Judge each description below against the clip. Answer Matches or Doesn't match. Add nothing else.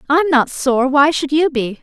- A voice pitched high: Matches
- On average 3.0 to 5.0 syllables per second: Matches